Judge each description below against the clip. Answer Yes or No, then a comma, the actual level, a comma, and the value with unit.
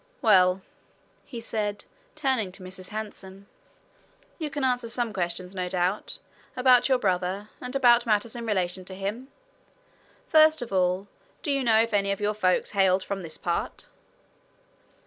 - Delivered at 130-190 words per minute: Yes, average, 155 wpm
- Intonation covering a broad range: No, average, 4.5 semitones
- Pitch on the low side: No, high, 205 Hz